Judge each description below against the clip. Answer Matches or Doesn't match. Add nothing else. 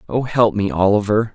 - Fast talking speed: Doesn't match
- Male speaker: Matches